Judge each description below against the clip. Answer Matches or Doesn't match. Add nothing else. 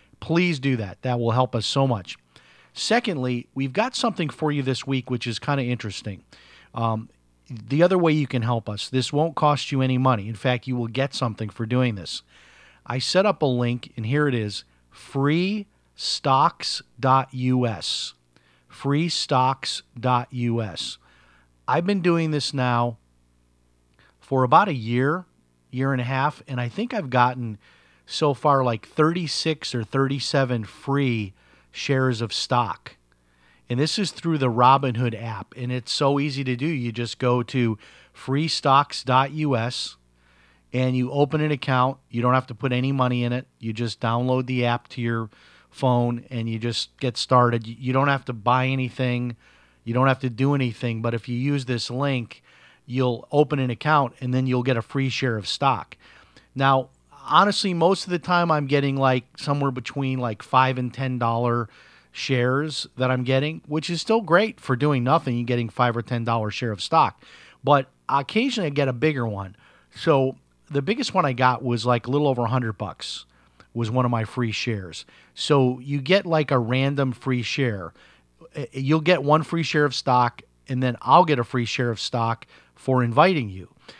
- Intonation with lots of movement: Doesn't match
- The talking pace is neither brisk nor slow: Matches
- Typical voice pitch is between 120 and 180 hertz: Matches